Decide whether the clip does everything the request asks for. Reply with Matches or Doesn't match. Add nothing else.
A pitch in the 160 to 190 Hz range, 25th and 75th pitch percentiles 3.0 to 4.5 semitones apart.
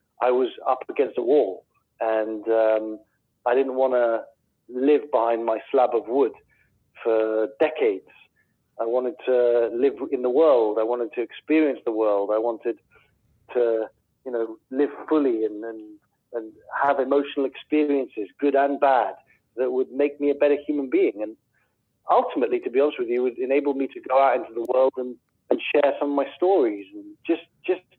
Doesn't match